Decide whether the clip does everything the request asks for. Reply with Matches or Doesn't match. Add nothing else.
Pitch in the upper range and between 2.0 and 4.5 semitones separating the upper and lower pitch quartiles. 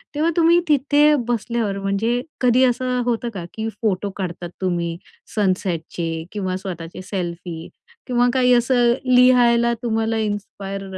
Doesn't match